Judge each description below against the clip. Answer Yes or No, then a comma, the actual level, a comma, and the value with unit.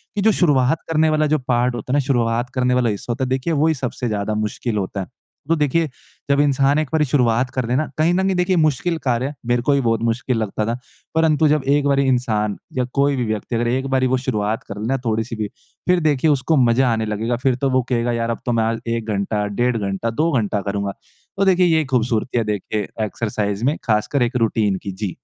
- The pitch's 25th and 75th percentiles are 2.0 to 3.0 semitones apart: No, average, 4.3 semitones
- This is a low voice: Yes, low, 125 Hz